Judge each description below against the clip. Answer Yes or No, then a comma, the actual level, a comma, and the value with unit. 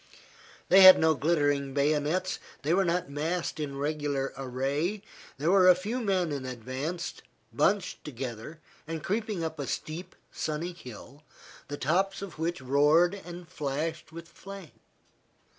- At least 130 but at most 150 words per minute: Yes, average, 140 wpm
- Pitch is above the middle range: No, medium, 160 Hz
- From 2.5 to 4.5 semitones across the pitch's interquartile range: Yes, average, 4.1 semitones